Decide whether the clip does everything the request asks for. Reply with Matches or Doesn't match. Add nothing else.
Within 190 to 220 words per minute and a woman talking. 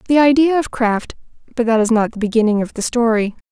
Matches